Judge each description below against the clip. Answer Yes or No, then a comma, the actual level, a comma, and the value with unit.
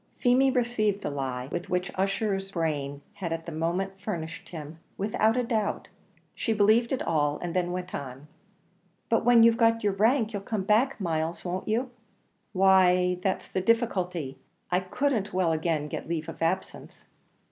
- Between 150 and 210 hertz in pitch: Yes, high, 190 Hz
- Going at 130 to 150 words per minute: No, average, 170 wpm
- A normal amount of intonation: Yes, average, 4.9 semitones